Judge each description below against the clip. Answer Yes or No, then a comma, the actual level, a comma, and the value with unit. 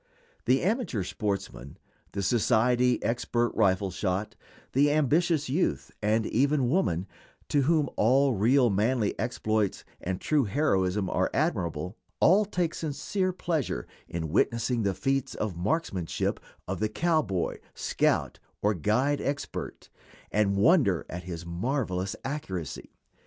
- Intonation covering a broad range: Yes, wide, 6.9 semitones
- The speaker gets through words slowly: Yes, slow, 125 wpm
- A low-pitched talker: Yes, low, 115 Hz